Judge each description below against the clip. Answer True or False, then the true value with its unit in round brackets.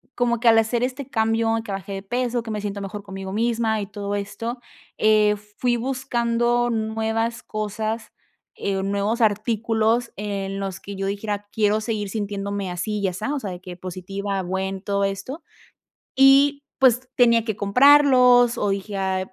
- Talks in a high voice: True (215 Hz)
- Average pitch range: True (3.0 semitones)